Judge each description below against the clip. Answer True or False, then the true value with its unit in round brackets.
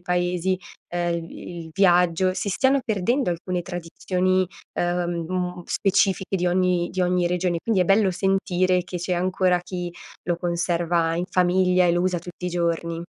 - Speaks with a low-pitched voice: False (180 Hz)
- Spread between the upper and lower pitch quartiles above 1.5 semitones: False (1.2 semitones)